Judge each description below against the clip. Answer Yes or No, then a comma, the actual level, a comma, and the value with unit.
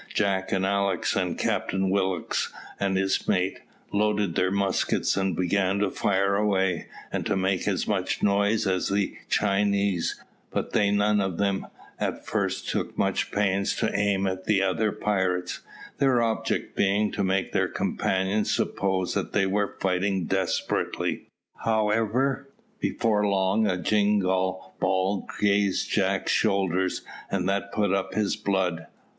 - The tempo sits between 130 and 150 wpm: Yes, average, 145 wpm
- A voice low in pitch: Yes, low, 100 Hz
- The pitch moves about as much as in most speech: No, narrow, 1.4 semitones